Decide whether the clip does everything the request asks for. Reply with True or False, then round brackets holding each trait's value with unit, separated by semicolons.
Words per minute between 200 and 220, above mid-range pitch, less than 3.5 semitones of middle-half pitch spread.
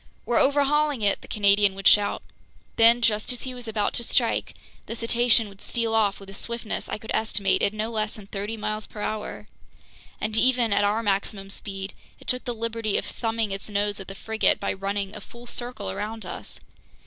True (205 wpm; 215 Hz; 2.4 semitones)